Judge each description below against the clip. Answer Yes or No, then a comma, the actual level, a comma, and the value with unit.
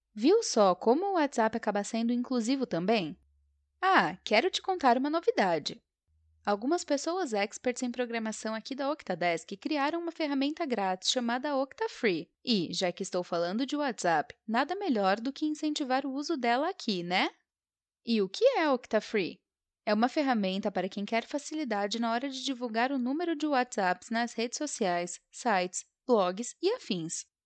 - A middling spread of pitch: No, wide, 6.1 semitones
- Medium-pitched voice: No, high, 240 Hz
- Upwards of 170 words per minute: No, average, 160 wpm